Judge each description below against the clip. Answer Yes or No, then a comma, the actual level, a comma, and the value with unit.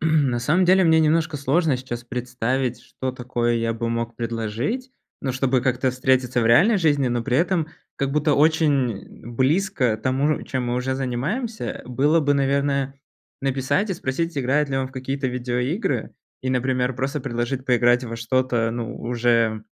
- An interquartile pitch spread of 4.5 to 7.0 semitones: No, average, 3.2 semitones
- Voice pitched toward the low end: Yes, low, 130 Hz